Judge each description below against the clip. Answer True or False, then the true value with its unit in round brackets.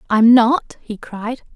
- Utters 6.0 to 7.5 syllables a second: False (3.3 syllables/s)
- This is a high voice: True (235 Hz)